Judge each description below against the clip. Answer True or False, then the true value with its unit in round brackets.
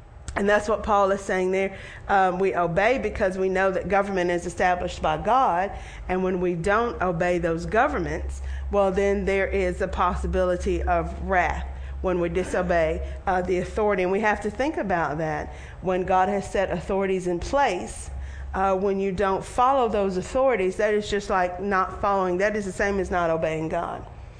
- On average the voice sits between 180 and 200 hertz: True (190 Hz)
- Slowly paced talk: False (185 wpm)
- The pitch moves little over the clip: True (2.0 semitones)